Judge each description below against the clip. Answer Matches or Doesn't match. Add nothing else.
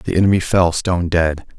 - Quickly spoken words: Doesn't match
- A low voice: Matches